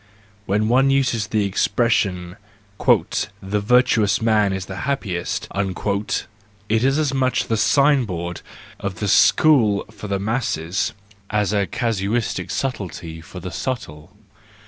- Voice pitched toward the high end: No, low, 105 Hz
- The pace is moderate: No, slow, 130 wpm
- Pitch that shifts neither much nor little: Yes, average, 3.9 semitones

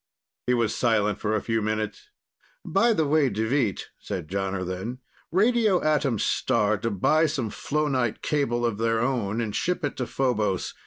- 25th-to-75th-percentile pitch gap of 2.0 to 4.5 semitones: No, average, 5.3 semitones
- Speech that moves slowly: No, average, 165 wpm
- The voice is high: No, low, 120 Hz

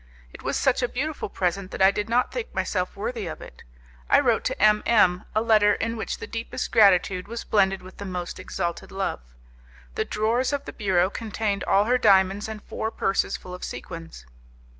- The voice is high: Yes, high, 205 Hz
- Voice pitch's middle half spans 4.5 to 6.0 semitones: No, average, 3.4 semitones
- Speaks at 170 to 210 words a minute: Yes, average, 200 wpm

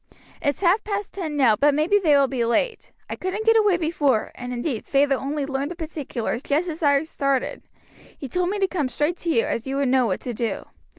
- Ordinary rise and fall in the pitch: Yes, average, 4.9 semitones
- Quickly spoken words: Yes, fast, 230 wpm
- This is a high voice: Yes, very high, 290 Hz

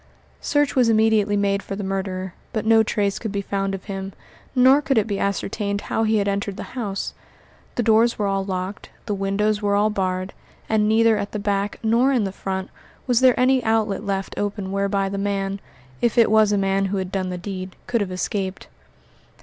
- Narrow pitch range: Yes, narrow, 2.1 semitones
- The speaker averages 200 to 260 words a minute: Yes, fast, 205 wpm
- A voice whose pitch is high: Yes, high, 200 Hz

